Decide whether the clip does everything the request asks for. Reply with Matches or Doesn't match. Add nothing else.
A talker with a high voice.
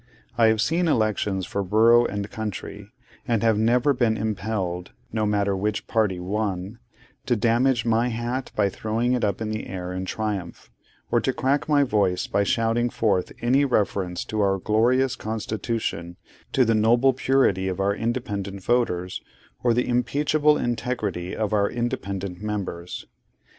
Doesn't match